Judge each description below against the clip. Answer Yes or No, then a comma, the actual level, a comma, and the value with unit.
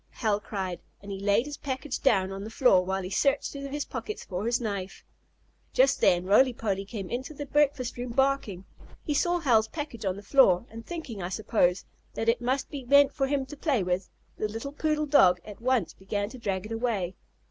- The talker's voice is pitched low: No, high, 230 Hz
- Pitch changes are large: Yes, wide, 5.8 semitones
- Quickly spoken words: Yes, fast, 215 wpm